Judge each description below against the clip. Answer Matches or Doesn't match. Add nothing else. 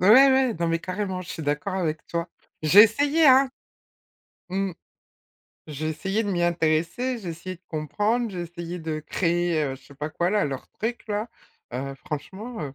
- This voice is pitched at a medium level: Matches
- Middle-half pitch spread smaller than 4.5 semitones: Doesn't match